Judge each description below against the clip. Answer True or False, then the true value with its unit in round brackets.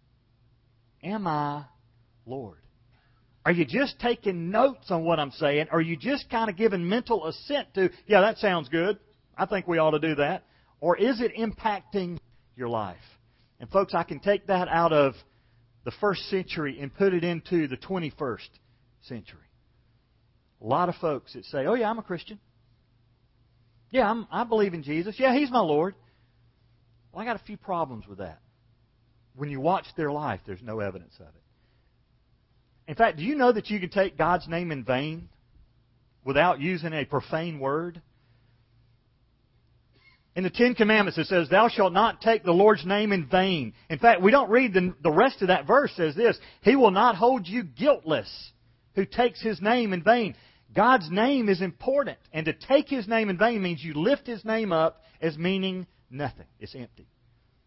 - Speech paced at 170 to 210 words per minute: True (185 wpm)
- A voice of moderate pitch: True (165 Hz)